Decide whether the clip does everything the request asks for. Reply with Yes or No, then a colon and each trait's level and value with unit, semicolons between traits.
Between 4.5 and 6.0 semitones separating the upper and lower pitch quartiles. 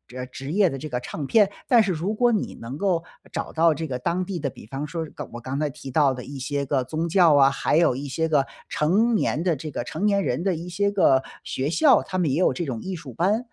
Yes: average, 5.3 semitones